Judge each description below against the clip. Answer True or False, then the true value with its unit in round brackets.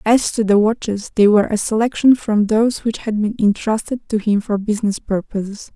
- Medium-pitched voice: False (215 Hz)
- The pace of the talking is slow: False (200 wpm)